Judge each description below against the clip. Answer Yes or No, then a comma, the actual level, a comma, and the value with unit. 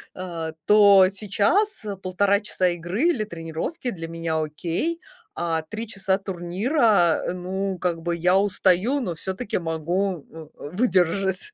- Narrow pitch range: No, average, 3.2 semitones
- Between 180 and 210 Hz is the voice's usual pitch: Yes, medium, 185 Hz